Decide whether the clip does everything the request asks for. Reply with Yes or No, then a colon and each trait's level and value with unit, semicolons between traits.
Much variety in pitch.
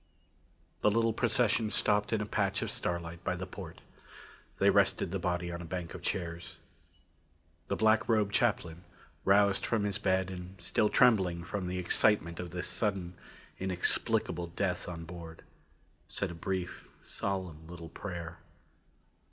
No: average, 3.1 semitones